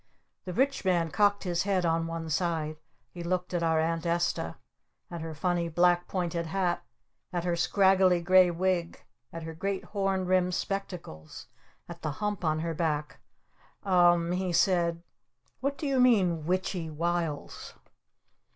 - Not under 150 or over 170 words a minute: Yes, average, 160 wpm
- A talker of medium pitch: Yes, medium, 175 Hz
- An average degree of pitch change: No, narrow, 2.1 semitones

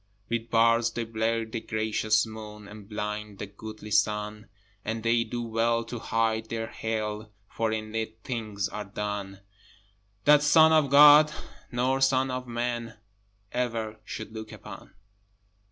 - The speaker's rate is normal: Yes, average, 145 wpm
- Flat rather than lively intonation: Yes, narrow, 1.7 semitones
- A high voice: No, low, 110 Hz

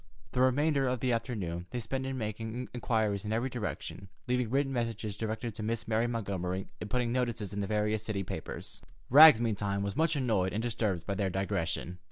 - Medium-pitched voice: No, low, 110 Hz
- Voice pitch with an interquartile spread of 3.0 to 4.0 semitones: Yes, average, 3.7 semitones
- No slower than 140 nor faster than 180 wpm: No, average, 195 wpm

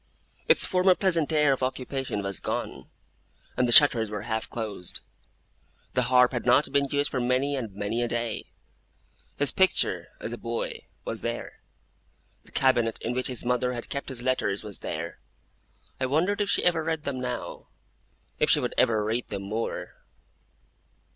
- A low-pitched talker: Yes, low, 125 Hz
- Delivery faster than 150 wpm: Yes, average, 170 wpm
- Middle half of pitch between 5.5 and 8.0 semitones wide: No, average, 4.0 semitones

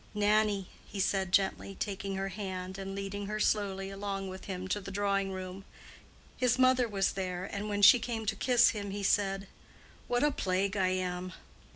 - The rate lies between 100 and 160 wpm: No, average, 185 wpm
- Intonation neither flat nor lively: No, narrow, 1.5 semitones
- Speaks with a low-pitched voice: No, high, 195 Hz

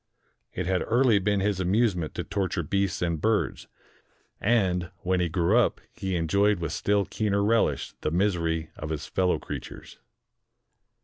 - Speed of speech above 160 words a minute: No, average, 150 wpm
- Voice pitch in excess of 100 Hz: No, very low, 95 Hz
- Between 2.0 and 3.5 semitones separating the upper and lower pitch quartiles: Yes, average, 3.2 semitones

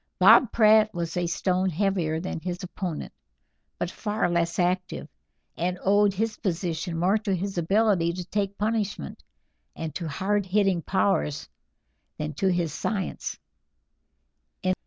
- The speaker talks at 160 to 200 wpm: No, slow, 135 wpm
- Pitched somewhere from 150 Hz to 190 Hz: Yes, medium, 185 Hz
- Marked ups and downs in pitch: No, average, 3.1 semitones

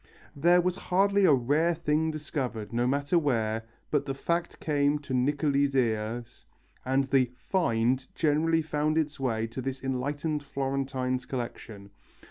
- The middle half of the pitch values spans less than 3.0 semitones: No, average, 3.5 semitones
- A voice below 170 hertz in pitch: Yes, medium, 140 Hz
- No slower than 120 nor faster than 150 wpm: Yes, average, 140 wpm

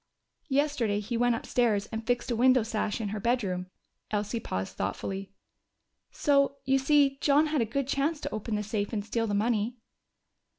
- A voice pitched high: Yes, high, 230 Hz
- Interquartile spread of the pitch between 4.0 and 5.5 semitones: Yes, average, 4.5 semitones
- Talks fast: No, average, 175 wpm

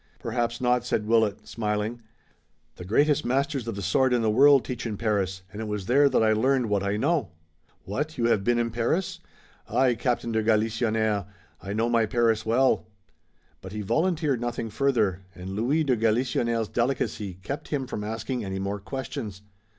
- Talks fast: No, average, 180 wpm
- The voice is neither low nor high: No, low, 115 Hz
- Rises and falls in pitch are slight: No, average, 3.4 semitones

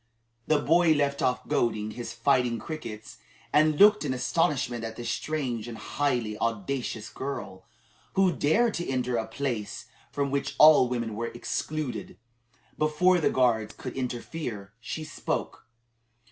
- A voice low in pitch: Yes, low, 130 Hz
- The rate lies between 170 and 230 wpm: No, average, 140 wpm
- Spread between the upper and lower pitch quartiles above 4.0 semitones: Yes, average, 4.8 semitones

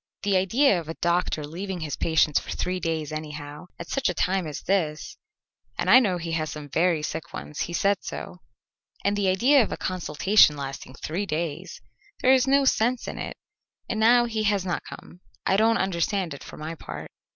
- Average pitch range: Yes, average, 4.7 semitones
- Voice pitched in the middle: Yes, medium, 180 Hz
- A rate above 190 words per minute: Yes, average, 200 wpm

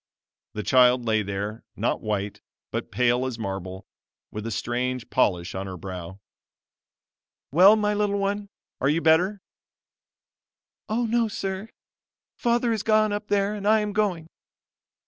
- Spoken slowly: No, average, 145 wpm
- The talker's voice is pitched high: No, medium, 160 Hz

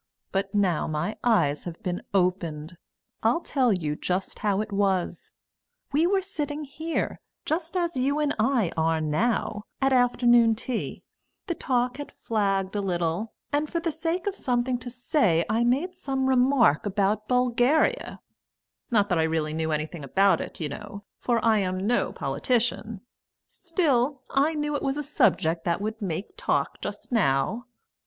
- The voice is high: Yes, high, 225 Hz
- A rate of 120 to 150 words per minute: No, average, 160 wpm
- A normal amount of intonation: No, wide, 6.8 semitones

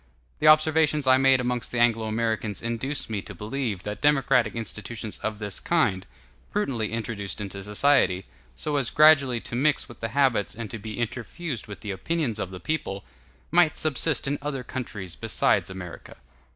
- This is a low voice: Yes, low, 120 Hz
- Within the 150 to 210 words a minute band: Yes, average, 170 wpm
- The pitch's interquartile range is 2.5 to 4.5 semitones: No, average, 5.1 semitones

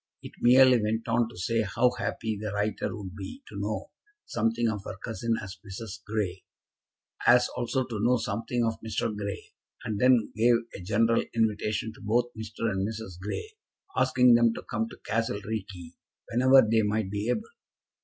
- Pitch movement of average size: No, narrow, 2.3 semitones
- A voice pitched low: Yes, low, 110 Hz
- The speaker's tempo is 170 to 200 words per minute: Yes, average, 175 wpm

